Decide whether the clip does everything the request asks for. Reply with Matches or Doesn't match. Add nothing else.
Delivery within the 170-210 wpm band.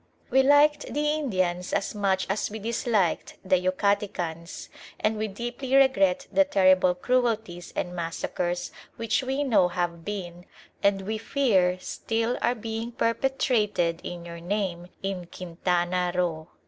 Doesn't match